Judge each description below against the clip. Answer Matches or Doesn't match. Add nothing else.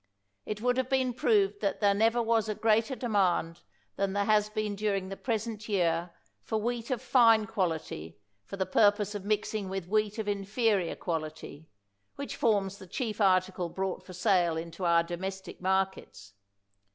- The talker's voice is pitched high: Matches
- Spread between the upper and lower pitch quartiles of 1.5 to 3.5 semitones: Matches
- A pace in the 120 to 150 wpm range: Doesn't match